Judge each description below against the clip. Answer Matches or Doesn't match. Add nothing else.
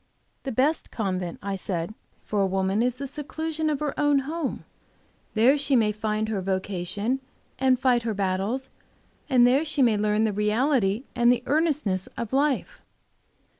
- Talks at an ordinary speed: Matches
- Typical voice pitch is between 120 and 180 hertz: Doesn't match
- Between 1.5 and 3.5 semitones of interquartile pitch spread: Doesn't match